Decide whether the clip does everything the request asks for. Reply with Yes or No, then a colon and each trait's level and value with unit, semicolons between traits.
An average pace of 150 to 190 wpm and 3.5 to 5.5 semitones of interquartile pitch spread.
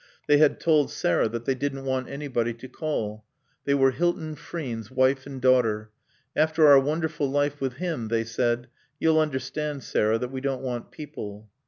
Yes: average, 175 wpm; average, 3.9 semitones